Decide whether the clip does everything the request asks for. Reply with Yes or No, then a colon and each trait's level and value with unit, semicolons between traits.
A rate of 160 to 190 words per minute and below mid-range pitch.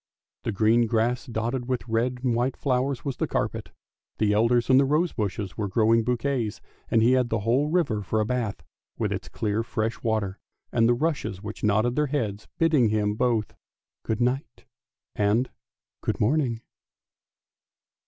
Yes: average, 175 wpm; low, 115 Hz